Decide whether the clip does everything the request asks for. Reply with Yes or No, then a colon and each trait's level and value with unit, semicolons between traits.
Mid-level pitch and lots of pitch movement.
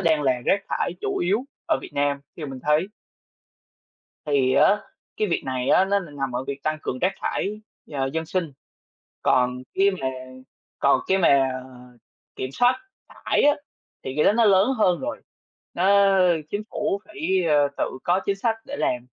Yes: medium, 170 Hz; wide, 6.3 semitones